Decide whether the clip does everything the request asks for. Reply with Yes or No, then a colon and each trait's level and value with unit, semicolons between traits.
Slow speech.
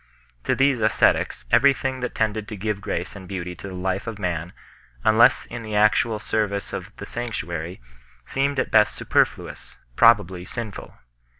No: average, 165 wpm